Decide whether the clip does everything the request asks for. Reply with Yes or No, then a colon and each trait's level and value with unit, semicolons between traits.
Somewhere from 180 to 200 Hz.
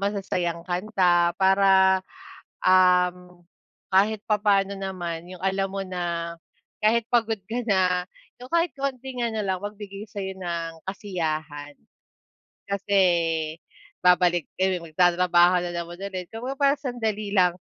Yes: high, 190 Hz